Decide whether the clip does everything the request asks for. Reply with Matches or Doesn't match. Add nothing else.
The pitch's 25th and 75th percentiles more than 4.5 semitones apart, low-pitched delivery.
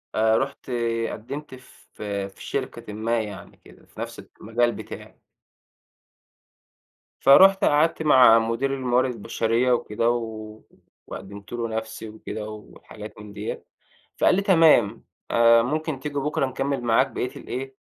Doesn't match